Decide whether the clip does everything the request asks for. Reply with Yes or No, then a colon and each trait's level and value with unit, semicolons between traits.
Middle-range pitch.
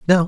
Yes: medium, 175 Hz